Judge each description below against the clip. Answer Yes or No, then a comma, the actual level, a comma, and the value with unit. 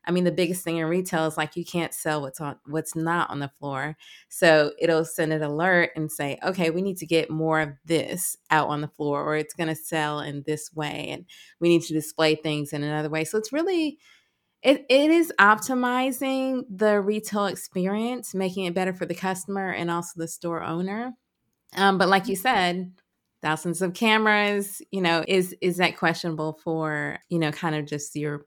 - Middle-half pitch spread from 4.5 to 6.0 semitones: No, average, 3.8 semitones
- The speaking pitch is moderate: Yes, medium, 170 Hz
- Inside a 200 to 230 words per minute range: Yes, fast, 205 wpm